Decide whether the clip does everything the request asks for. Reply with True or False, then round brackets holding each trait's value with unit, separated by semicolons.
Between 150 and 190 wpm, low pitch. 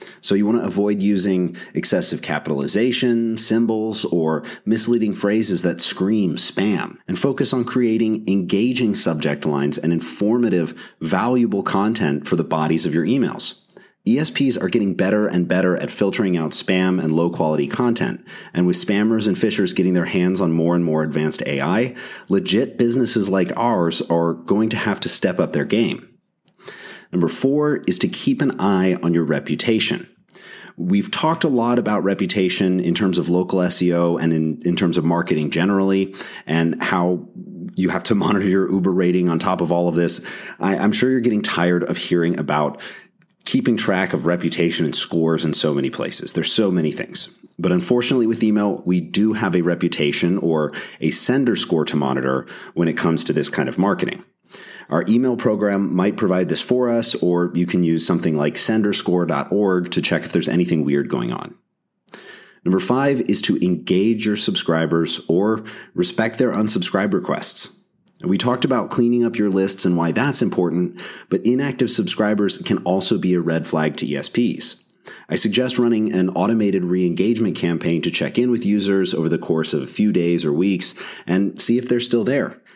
True (180 wpm; 95 Hz)